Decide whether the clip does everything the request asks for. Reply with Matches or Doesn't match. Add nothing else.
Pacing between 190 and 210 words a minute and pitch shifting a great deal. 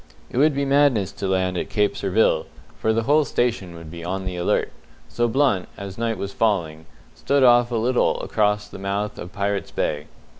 Doesn't match